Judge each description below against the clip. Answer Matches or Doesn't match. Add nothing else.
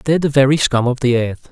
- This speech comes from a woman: Doesn't match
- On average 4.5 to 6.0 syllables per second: Doesn't match